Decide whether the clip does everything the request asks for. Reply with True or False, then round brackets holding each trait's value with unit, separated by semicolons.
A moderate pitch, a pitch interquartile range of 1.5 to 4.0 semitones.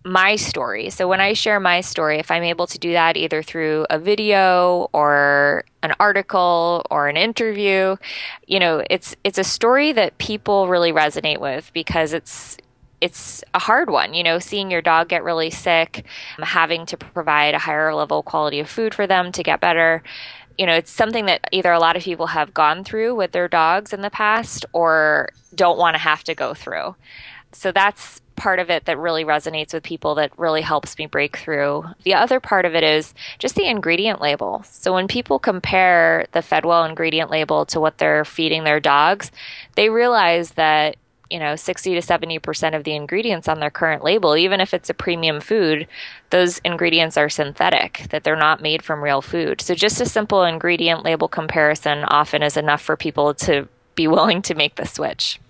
True (165 Hz; 3.3 semitones)